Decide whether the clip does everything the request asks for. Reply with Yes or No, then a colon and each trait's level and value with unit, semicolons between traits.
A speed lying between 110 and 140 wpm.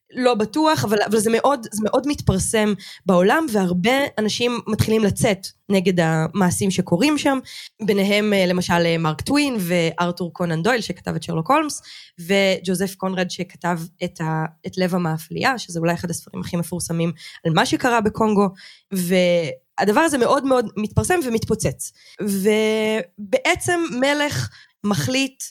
Yes: average, 130 wpm